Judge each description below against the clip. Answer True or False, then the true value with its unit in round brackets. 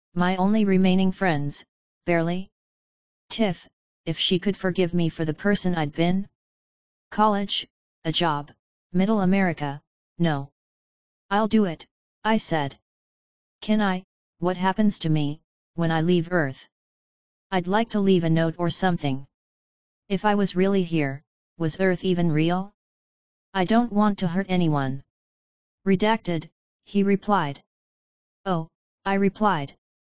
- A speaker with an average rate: False (130 wpm)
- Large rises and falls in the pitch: False (3.5 semitones)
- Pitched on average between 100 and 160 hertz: False (180 Hz)